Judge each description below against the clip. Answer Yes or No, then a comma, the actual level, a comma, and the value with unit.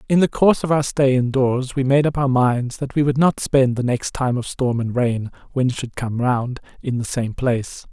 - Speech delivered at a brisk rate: Yes, fast, 260 wpm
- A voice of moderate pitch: No, low, 130 Hz